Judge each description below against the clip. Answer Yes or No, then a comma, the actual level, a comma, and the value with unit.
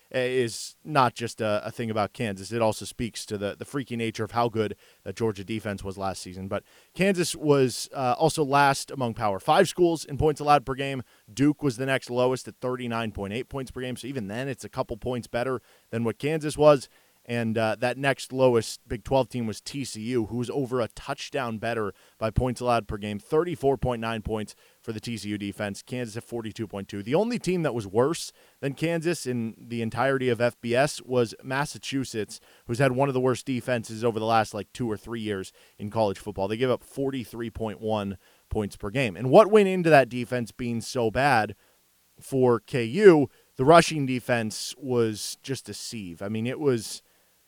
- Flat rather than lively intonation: No, average, 3.5 semitones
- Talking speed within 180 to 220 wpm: Yes, average, 195 wpm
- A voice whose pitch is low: Yes, low, 120 Hz